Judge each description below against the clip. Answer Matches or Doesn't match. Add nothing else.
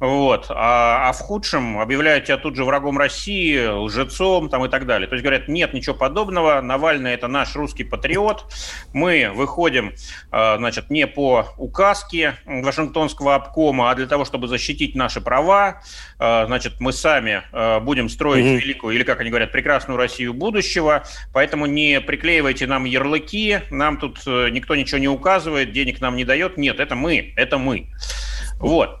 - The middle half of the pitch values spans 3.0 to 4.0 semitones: Matches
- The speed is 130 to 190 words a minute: Matches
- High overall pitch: Doesn't match